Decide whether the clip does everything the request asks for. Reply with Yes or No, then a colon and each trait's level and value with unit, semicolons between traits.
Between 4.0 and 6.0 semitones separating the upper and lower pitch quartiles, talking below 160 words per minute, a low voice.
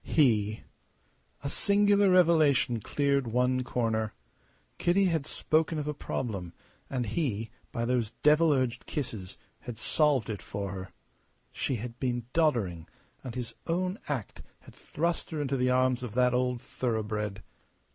Yes: average, 5.1 semitones; average, 145 wpm; low, 125 Hz